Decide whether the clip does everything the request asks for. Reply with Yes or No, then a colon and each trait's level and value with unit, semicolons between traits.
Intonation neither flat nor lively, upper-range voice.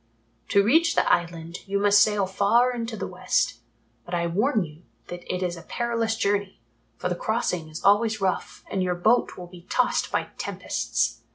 Yes: average, 4.0 semitones; high, 200 Hz